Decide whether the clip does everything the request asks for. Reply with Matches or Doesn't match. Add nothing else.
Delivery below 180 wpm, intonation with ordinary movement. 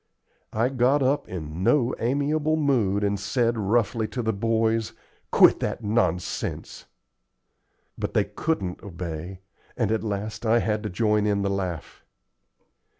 Matches